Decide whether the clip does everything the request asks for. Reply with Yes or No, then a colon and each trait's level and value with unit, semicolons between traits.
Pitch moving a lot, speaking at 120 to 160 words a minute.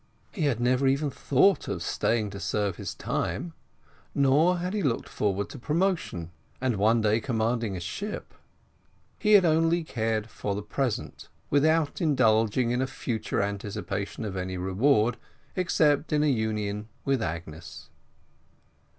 Yes: wide, 6.3 semitones; average, 145 wpm